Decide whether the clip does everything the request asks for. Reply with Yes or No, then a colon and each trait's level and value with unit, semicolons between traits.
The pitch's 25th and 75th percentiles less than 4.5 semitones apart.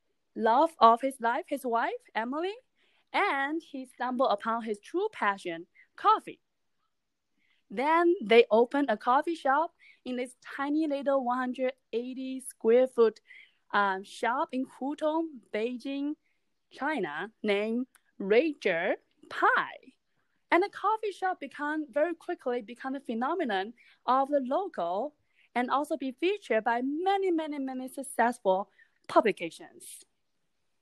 No: average, 5.3 semitones